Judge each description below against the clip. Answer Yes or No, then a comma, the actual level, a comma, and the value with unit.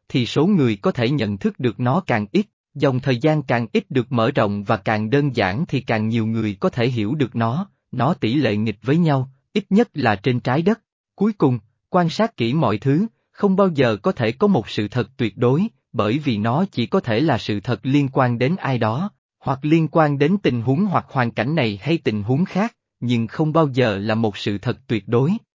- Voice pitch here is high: No, low, 130 Hz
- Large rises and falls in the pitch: Yes, wide, 6.2 semitones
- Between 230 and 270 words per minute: Yes, average, 235 wpm